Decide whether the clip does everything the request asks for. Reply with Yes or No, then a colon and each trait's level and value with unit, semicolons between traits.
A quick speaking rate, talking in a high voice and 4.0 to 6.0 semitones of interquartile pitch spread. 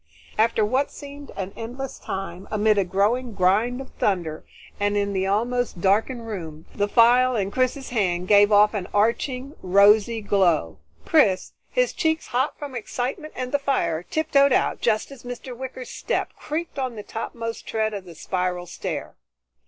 No: average, 165 wpm; high, 220 Hz; average, 4.5 semitones